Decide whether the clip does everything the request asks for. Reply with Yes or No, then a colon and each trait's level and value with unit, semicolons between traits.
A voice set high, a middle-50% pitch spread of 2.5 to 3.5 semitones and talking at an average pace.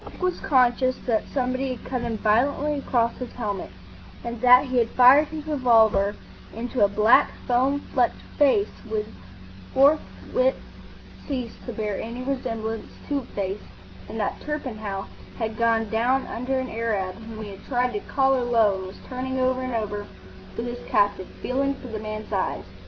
Yes: high, 240 Hz; average, 3.2 semitones; average, 170 wpm